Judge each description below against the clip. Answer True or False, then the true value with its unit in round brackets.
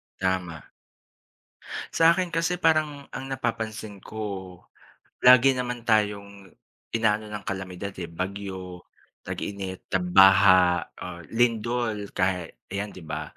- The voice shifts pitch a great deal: False (4.1 semitones)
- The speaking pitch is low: True (100 Hz)